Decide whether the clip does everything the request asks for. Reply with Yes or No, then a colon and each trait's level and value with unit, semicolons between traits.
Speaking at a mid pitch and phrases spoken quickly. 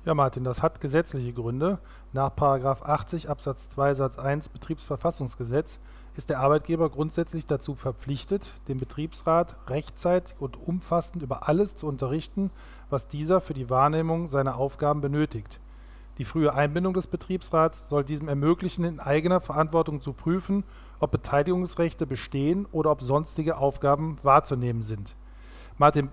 No: medium, 145 Hz; average, 135 wpm